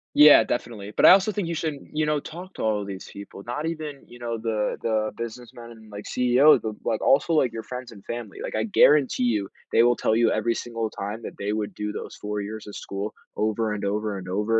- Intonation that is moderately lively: Yes, average, 3.1 semitones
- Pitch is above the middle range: No, low, 115 Hz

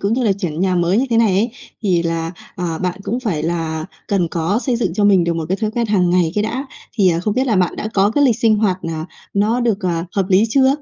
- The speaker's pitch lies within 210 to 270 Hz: No, high, 195 Hz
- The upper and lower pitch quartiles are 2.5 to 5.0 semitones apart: Yes, average, 4.4 semitones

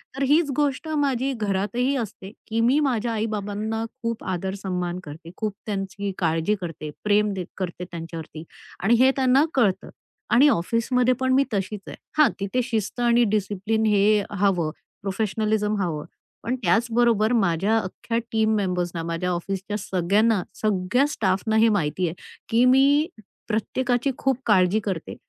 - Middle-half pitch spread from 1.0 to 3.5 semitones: No, average, 4.2 semitones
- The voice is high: Yes, high, 210 Hz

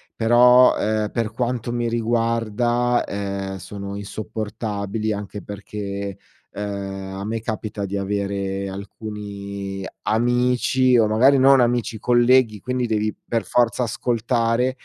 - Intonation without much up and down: No, average, 3.1 semitones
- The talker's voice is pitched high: No, low, 110 Hz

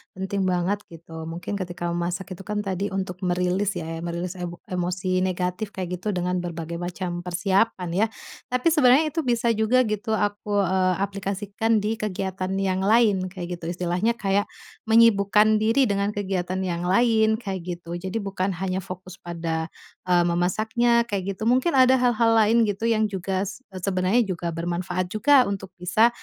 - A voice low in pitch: No, high, 190 Hz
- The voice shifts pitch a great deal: No, average, 3.3 semitones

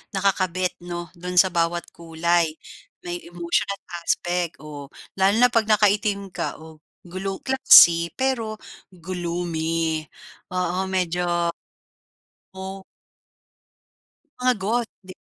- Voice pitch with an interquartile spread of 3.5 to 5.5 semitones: No, narrow, 2.5 semitones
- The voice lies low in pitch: No, medium, 180 Hz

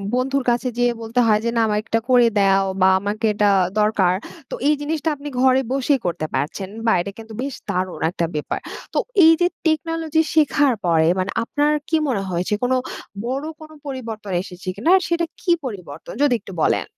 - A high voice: Yes, high, 235 Hz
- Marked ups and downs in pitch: Yes, wide, 6.5 semitones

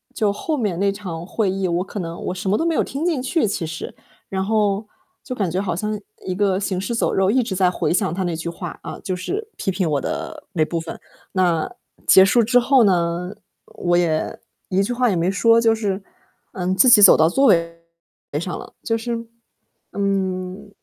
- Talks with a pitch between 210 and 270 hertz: No, high, 195 Hz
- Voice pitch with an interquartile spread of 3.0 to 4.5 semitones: Yes, average, 3.8 semitones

